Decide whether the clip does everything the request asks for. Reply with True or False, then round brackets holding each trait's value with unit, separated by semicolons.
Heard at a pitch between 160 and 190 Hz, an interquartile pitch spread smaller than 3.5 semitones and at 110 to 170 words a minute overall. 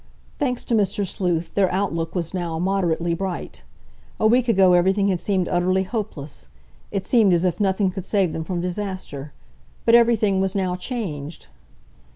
True (185 Hz; 2.7 semitones; 165 wpm)